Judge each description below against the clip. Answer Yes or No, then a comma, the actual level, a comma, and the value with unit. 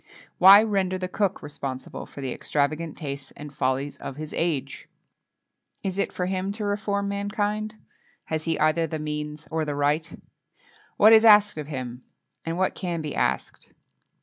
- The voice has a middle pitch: Yes, medium, 165 Hz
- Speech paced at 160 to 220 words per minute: Yes, average, 165 wpm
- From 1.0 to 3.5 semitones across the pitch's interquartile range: No, average, 5.3 semitones